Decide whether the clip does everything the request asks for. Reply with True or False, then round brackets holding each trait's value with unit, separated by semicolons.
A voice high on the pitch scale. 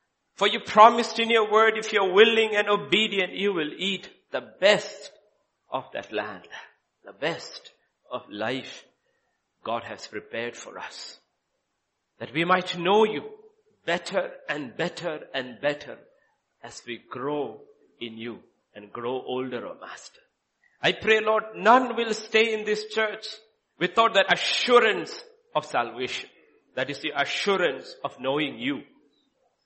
True (215 Hz)